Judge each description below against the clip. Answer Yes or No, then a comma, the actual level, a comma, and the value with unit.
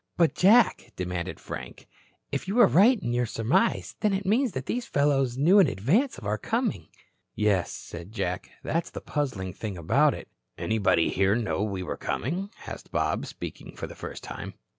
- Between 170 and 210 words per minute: Yes, average, 185 wpm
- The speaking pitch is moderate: No, low, 130 Hz